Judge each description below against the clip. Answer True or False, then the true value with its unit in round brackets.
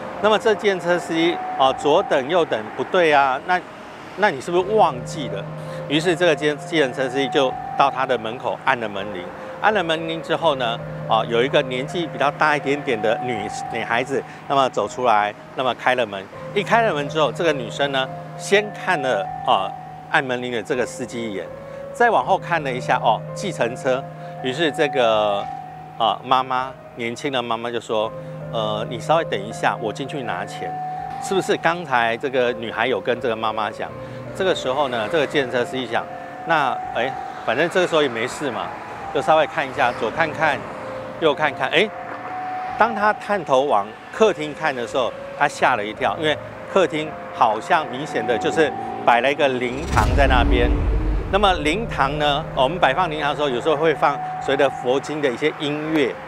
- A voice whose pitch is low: False (155 Hz)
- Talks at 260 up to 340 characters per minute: True (280 characters per minute)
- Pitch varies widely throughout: True (7.8 semitones)